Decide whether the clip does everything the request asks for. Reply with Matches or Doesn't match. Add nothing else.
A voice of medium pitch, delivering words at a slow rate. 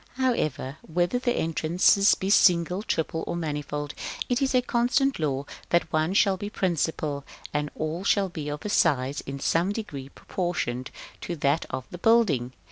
Doesn't match